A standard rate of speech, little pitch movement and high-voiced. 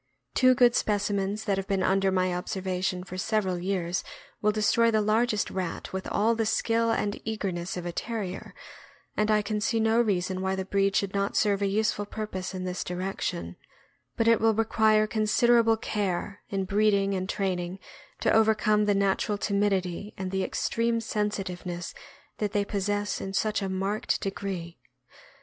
Yes: average, 170 wpm; narrow, 2.3 semitones; high, 200 Hz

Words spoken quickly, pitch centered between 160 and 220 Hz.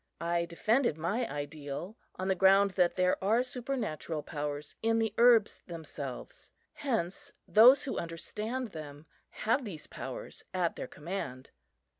No: slow, 135 wpm; high, 190 Hz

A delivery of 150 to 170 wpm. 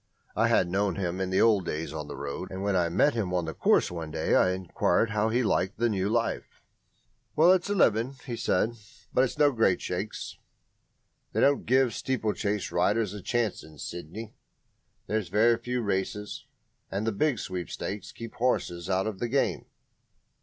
No: average, 185 wpm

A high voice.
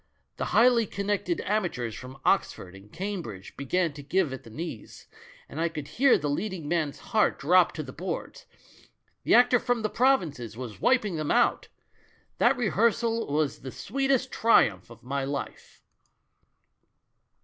No: medium, 170 Hz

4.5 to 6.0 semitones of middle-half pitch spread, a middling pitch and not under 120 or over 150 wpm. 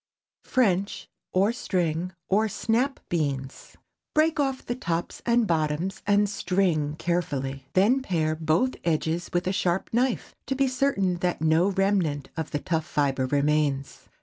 Yes: average, 5.1 semitones; medium, 175 Hz; average, 145 wpm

